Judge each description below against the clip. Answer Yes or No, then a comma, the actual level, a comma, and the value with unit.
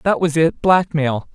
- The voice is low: No, medium, 160 Hz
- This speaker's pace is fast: No, slow, 135 wpm